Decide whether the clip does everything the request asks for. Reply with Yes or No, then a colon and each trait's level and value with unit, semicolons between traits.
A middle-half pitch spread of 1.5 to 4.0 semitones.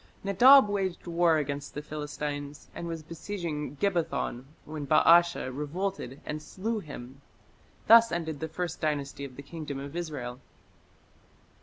Yes: average, 3.5 semitones